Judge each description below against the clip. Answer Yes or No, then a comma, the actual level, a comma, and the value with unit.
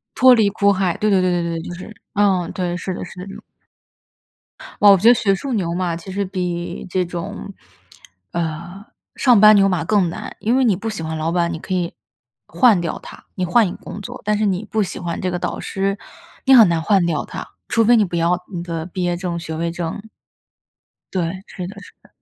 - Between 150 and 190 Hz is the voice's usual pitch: Yes, medium, 185 Hz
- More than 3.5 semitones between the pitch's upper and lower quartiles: No, average, 3.0 semitones